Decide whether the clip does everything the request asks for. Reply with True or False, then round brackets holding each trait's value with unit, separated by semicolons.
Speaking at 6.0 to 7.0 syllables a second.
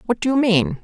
True (6.4 syllables/s)